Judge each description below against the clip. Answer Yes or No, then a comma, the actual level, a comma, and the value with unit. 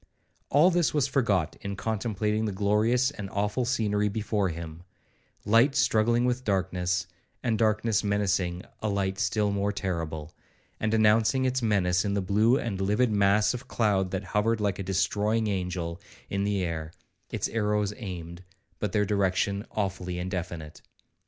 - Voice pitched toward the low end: Yes, low, 100 Hz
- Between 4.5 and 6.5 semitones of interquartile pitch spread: No, average, 2.9 semitones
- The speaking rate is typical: Yes, average, 145 wpm